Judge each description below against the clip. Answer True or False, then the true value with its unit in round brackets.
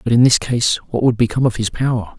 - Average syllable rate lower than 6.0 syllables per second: False (6.1 syllables/s)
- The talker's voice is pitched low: True (120 Hz)